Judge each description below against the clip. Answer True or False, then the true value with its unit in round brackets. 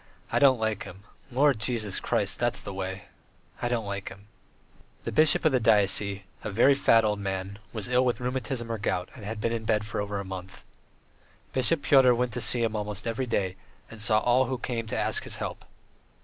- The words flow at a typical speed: False (215 wpm)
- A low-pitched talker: True (110 Hz)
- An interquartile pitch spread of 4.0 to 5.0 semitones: False (3.5 semitones)